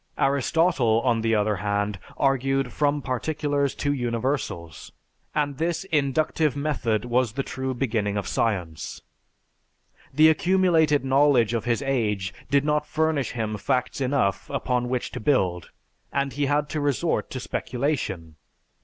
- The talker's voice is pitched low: Yes, low, 130 Hz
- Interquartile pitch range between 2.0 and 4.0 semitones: No, average, 4.4 semitones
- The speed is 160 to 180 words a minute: No, slow, 135 wpm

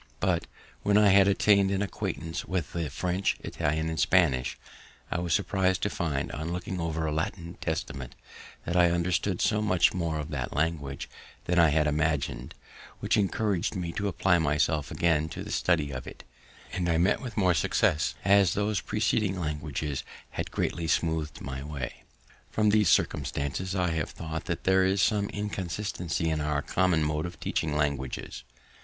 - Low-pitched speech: Yes, very low, 85 Hz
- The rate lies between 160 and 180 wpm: Yes, average, 170 wpm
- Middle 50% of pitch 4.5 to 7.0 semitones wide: No, average, 3.8 semitones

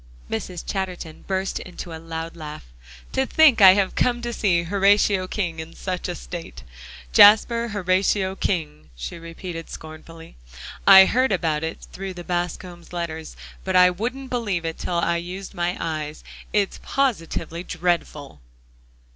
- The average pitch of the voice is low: No, medium, 180 Hz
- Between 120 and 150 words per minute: Yes, average, 145 wpm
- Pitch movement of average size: Yes, average, 3.0 semitones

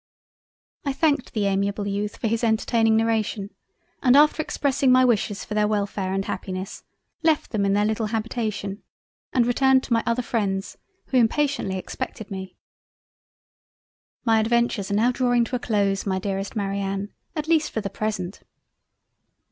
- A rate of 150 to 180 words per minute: Yes, average, 155 wpm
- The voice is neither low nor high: No, high, 220 Hz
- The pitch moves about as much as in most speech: Yes, average, 3.5 semitones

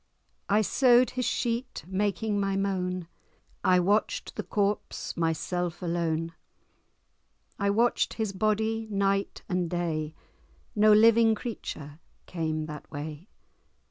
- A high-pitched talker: Yes, high, 195 Hz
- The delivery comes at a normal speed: No, slow, 110 wpm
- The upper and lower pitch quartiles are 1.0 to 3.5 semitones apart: No, average, 4.2 semitones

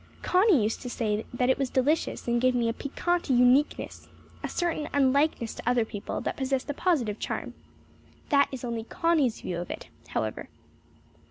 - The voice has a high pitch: Yes, very high, 255 Hz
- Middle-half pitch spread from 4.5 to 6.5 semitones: No, average, 3.9 semitones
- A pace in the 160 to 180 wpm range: Yes, average, 175 wpm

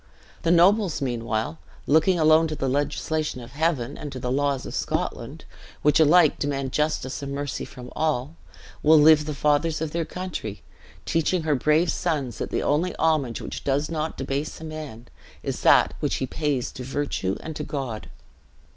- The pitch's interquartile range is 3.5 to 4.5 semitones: No, average, 3.1 semitones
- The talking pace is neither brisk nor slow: Yes, average, 175 wpm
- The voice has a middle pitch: Yes, medium, 150 Hz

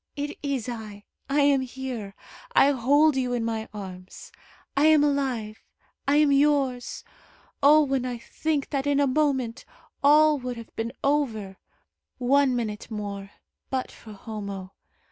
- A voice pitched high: Yes, very high, 260 Hz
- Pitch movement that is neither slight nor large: Yes, average, 4.3 semitones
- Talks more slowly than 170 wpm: Yes, average, 145 wpm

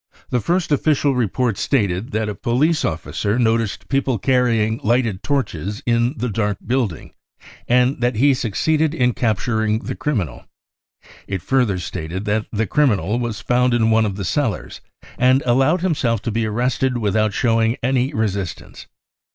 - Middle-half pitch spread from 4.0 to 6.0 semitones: No, average, 3.4 semitones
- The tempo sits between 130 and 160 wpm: Yes, average, 155 wpm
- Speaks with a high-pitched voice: No, low, 115 Hz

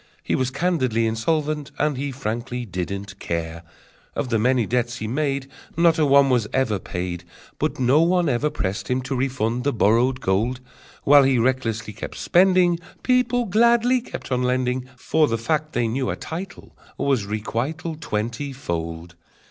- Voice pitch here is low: Yes, low, 130 Hz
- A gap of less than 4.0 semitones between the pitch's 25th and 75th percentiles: No, average, 5.1 semitones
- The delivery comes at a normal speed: Yes, average, 165 wpm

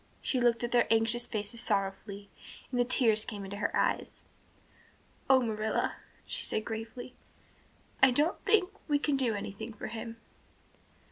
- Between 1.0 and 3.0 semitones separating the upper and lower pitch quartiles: Yes, average, 2.7 semitones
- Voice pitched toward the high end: Yes, high, 230 Hz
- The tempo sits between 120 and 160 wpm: Yes, average, 150 wpm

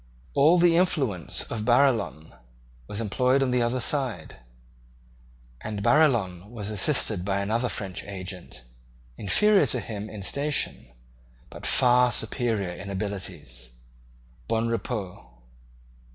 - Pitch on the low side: Yes, low, 110 Hz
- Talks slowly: Yes, slow, 110 wpm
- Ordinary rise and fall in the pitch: Yes, average, 4.6 semitones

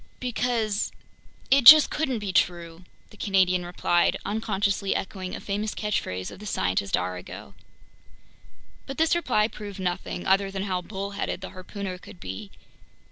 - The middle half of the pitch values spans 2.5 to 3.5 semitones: Yes, average, 2.9 semitones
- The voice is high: Yes, high, 195 Hz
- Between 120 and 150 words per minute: Yes, average, 140 wpm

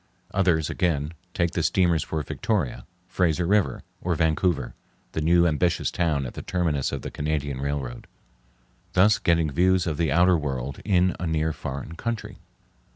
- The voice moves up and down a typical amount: Yes, average, 3.5 semitones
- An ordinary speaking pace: Yes, average, 155 wpm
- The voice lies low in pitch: Yes, very low, 85 Hz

